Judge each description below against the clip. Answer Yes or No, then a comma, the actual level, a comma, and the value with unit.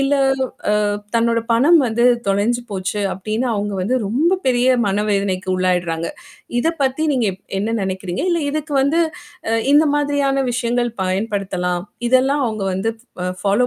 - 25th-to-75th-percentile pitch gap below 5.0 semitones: No, wide, 5.4 semitones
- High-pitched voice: Yes, high, 225 Hz